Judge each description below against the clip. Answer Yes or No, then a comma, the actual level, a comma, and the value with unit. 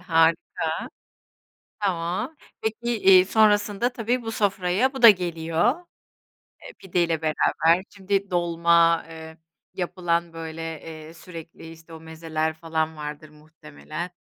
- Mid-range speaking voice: Yes, medium, 170 Hz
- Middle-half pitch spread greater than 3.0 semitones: Yes, average, 3.5 semitones